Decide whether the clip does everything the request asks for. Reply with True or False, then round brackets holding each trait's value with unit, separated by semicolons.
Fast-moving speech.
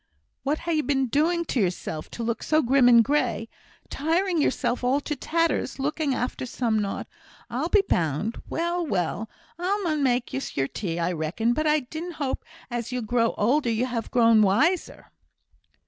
False (180 wpm)